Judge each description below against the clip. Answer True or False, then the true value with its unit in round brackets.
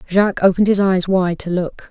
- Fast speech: True (220 wpm)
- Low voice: False (185 Hz)